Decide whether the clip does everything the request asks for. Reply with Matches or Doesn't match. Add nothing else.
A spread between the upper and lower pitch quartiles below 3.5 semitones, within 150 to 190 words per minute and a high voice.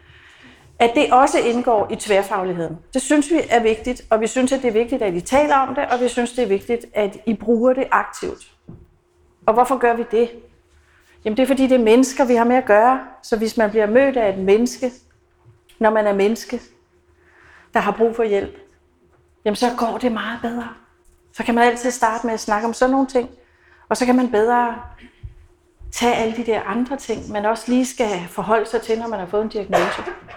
Doesn't match